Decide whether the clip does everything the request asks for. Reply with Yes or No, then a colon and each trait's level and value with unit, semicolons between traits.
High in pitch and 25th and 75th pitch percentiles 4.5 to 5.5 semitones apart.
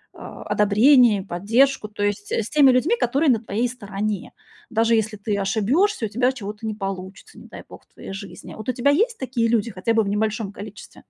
No: high, 220 Hz; average, 3.5 semitones